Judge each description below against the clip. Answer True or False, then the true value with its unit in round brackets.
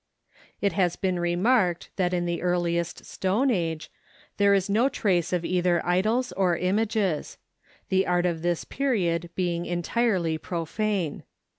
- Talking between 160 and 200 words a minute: False (140 wpm)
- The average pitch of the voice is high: False (180 Hz)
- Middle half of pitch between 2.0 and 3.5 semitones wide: True (2.7 semitones)